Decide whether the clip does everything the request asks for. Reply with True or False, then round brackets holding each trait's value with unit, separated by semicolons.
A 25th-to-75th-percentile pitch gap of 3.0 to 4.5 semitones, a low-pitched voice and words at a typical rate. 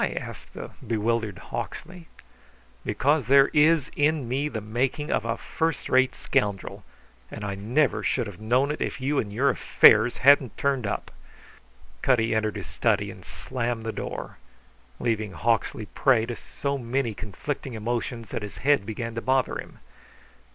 True (4.1 semitones; 120 Hz; 160 wpm)